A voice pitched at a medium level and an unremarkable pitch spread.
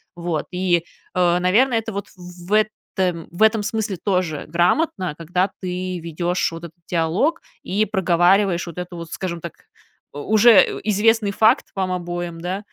Yes: medium, 180 Hz; average, 3.0 semitones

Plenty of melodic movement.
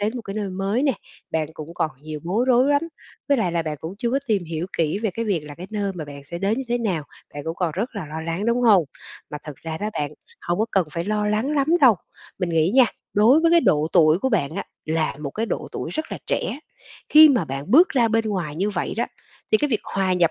Yes: wide, 6.1 semitones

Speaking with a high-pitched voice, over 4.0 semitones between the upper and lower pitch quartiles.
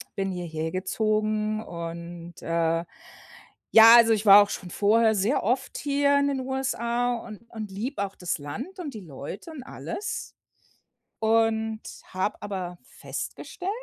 Yes: high, 215 Hz; average, 4.5 semitones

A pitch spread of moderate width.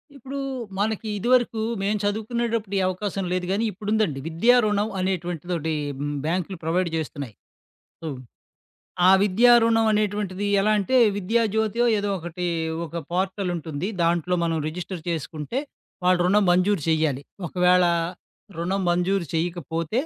Yes: average, 3.7 semitones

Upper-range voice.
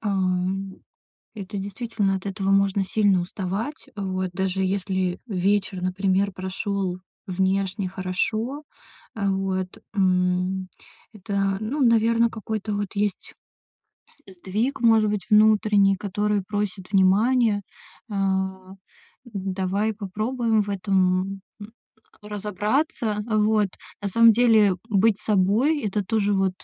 Yes: high, 200 Hz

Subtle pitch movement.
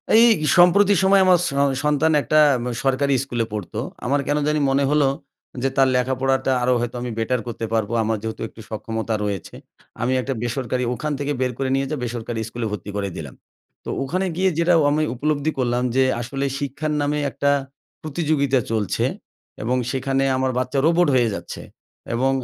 No: average, 3.7 semitones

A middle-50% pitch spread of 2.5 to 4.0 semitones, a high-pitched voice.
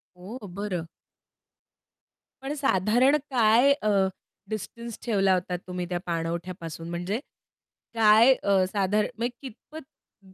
No: average, 4.6 semitones; high, 205 Hz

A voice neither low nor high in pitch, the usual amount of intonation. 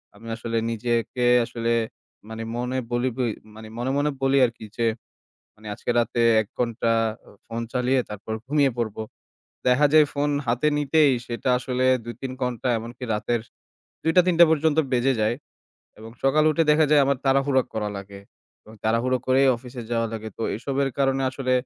No: low, 125 Hz; average, 3.0 semitones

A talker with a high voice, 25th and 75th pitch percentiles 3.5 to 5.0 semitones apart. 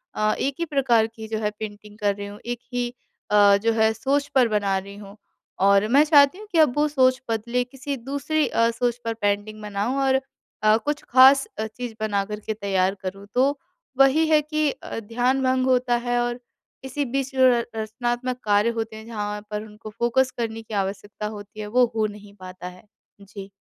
Yes: high, 230 Hz; average, 3.8 semitones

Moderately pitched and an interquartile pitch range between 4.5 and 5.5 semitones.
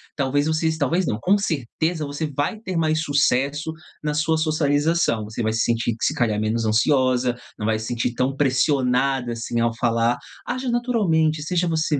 Yes: medium, 145 Hz; average, 5.0 semitones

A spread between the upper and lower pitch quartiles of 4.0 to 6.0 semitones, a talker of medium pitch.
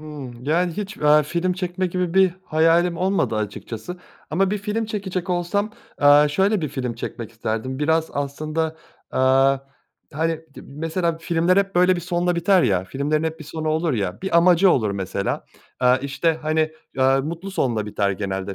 Yes: average, 5.1 semitones; medium, 160 Hz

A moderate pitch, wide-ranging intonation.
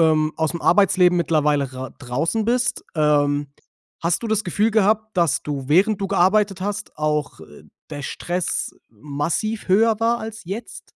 Yes: medium, 175 Hz; wide, 6.1 semitones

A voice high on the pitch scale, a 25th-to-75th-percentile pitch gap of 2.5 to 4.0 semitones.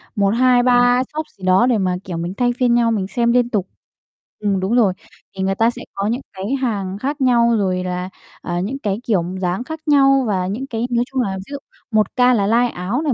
No: high, 230 Hz; average, 4.5 semitones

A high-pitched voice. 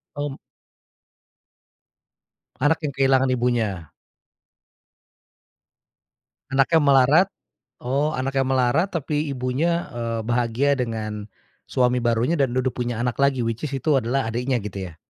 No: low, 130 Hz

